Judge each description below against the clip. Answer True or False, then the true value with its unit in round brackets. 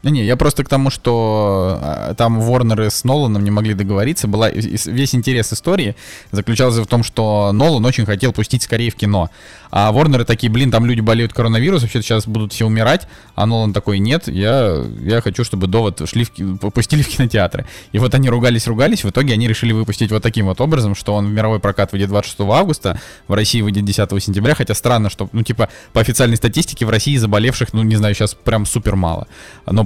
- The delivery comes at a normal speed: False (200 wpm)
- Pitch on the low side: True (115 Hz)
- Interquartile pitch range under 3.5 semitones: True (3.0 semitones)